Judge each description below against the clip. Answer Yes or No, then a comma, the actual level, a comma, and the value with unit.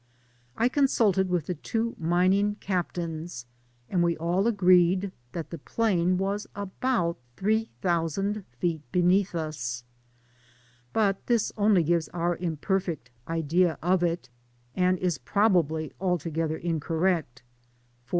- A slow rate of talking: Yes, slow, 120 wpm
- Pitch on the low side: No, medium, 180 Hz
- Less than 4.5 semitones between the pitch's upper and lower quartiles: Yes, average, 3.0 semitones